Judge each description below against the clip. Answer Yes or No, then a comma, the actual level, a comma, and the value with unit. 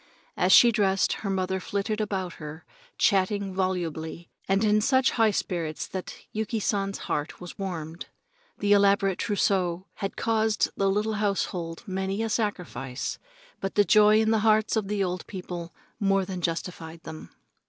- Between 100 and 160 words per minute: Yes, average, 155 wpm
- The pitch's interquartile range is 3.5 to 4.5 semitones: No, average, 2.9 semitones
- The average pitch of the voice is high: Yes, high, 195 Hz